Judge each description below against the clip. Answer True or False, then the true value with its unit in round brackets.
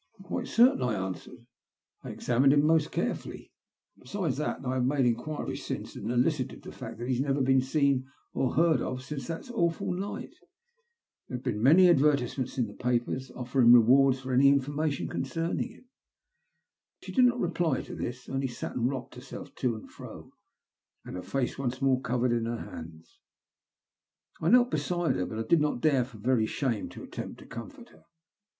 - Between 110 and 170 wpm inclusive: False (180 wpm)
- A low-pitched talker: True (130 Hz)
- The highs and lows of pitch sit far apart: False (3.7 semitones)